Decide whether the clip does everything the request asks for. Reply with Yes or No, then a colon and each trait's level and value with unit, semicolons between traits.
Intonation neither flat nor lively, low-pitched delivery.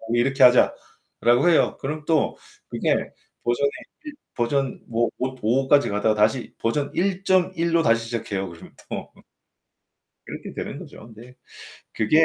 Yes: average, 4.7 semitones; low, 130 Hz